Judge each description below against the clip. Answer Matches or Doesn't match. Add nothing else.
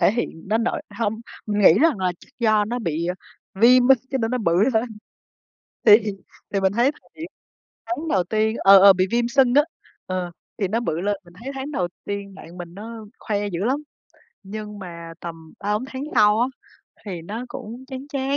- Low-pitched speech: Doesn't match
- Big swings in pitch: Doesn't match